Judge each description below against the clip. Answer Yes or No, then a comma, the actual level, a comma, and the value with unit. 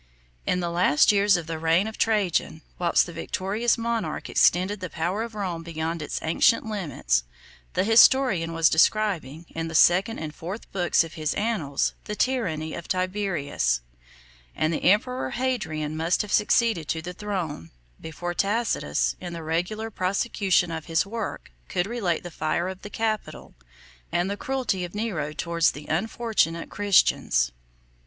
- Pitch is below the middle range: No, medium, 180 Hz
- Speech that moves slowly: No, average, 160 wpm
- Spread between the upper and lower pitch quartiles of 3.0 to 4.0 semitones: No, average, 4.5 semitones